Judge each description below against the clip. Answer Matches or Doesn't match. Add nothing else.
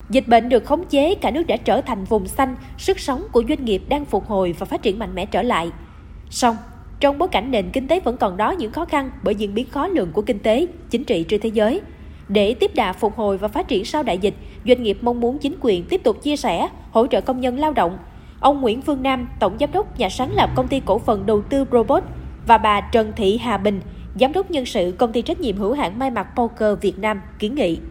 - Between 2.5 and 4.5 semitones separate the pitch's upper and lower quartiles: Doesn't match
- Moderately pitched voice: Doesn't match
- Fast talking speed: Matches